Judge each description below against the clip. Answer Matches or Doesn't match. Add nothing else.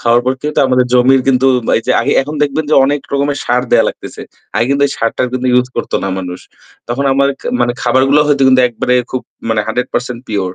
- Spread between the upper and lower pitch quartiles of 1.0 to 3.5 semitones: Matches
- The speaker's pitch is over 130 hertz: Doesn't match